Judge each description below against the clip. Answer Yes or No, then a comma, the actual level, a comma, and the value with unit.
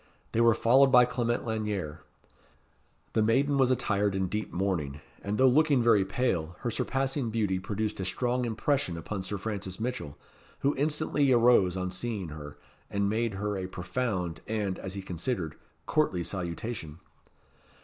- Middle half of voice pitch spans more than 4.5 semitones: Yes, average, 4.9 semitones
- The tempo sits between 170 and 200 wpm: No, average, 155 wpm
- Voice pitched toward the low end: Yes, low, 105 Hz